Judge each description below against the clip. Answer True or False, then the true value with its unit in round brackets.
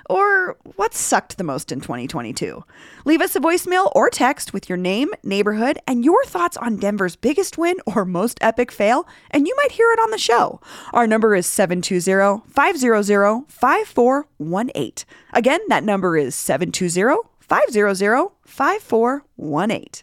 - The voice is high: True (240 Hz)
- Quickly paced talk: False (145 wpm)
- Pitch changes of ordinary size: False (9.0 semitones)